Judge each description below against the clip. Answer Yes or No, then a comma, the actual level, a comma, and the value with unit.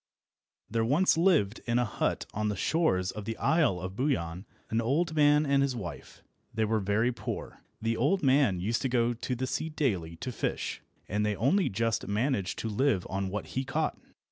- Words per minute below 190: No, average, 195 wpm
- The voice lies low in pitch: Yes, low, 115 Hz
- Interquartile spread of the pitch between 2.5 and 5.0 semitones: No, wide, 5.4 semitones